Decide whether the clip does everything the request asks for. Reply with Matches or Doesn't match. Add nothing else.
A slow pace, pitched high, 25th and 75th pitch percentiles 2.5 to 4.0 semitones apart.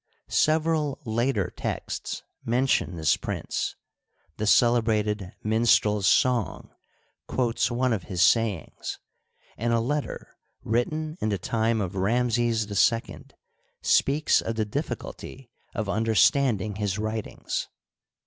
Doesn't match